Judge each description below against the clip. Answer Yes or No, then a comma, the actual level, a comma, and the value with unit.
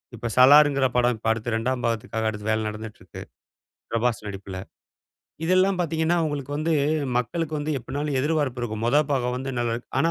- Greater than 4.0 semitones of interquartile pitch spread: Yes, average, 4.9 semitones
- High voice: No, low, 125 Hz